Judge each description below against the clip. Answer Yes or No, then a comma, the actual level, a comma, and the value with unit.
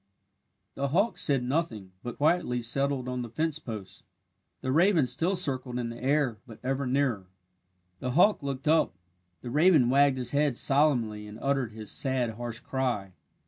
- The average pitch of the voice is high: No, low, 130 Hz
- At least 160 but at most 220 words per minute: Yes, average, 165 wpm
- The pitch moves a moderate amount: Yes, average, 3.4 semitones